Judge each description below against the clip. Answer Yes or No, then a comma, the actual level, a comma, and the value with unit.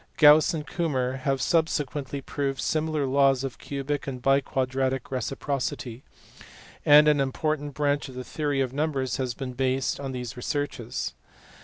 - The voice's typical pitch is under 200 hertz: Yes, low, 135 Hz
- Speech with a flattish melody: Yes, narrow, 2.0 semitones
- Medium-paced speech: Yes, average, 145 wpm